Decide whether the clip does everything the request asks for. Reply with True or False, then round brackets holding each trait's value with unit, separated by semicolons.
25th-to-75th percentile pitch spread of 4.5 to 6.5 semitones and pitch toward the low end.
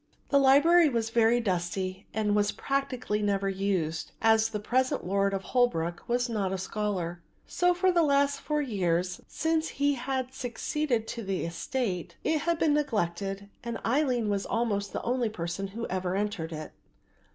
False (5.6 semitones; 220 Hz)